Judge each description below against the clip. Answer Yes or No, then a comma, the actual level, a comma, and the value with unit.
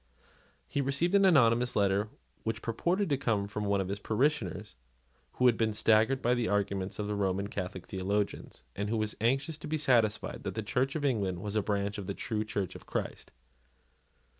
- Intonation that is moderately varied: Yes, average, 4.0 semitones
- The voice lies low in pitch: Yes, low, 110 Hz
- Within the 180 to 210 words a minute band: Yes, average, 190 wpm